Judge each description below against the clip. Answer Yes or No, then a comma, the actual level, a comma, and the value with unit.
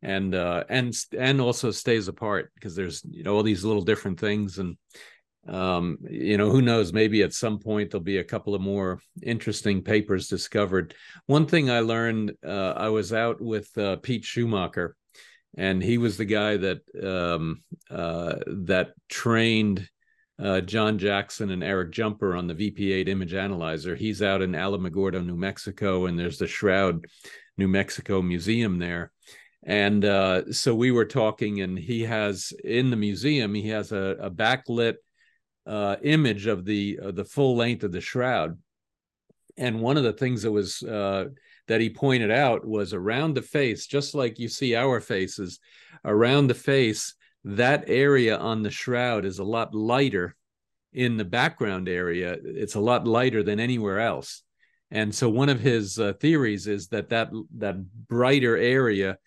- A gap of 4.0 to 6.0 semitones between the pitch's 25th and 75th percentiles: No, average, 3.5 semitones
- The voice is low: Yes, low, 105 Hz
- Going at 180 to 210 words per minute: No, average, 170 wpm